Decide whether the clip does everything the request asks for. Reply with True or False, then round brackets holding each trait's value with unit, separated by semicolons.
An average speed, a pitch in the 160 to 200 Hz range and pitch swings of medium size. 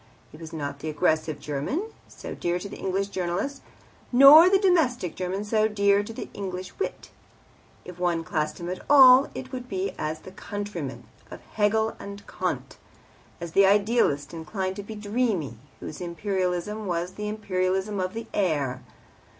True (165 wpm; 190 Hz; 4.0 semitones)